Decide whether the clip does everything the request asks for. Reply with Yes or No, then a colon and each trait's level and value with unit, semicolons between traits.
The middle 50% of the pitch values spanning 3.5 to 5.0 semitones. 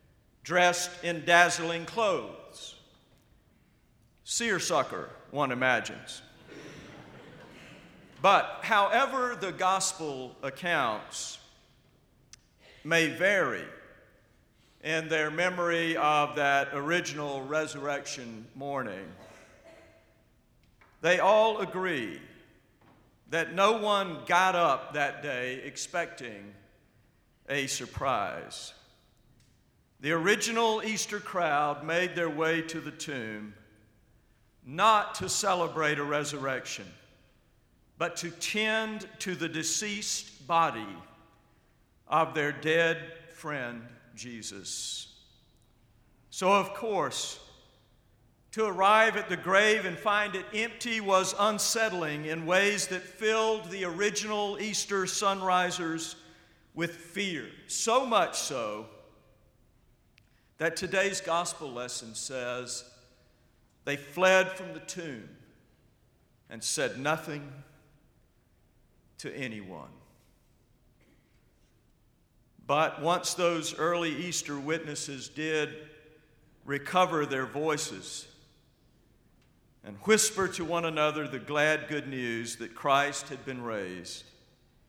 No: wide, 5.5 semitones